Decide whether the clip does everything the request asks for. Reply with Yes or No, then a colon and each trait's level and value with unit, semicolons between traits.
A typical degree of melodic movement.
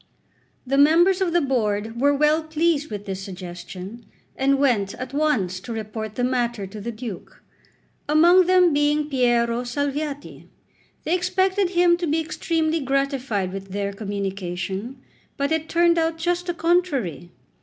No: wide, 7.4 semitones